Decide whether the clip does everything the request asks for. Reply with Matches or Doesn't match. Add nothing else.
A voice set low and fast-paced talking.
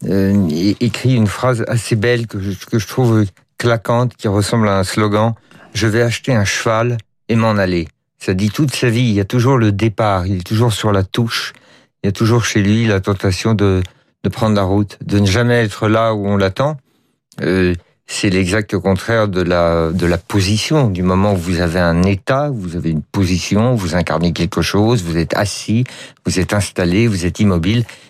Doesn't match